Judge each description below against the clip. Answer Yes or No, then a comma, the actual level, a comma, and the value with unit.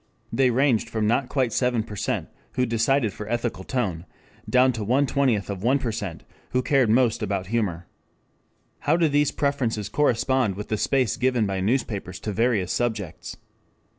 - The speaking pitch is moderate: No, low, 115 Hz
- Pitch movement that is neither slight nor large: Yes, average, 3.8 semitones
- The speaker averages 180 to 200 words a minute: No, average, 160 wpm